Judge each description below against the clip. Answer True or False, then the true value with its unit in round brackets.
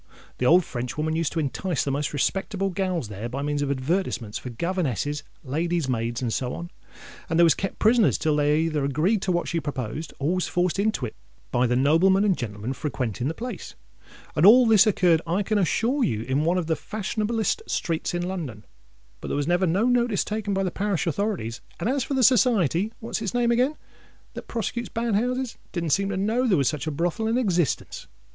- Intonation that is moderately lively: False (6.5 semitones)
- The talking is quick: True (210 wpm)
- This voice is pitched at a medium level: True (175 Hz)